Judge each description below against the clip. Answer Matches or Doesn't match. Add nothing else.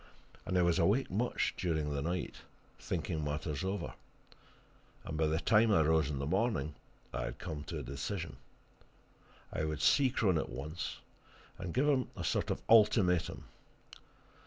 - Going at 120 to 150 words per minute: Doesn't match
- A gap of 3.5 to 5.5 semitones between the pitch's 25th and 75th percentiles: Matches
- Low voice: Matches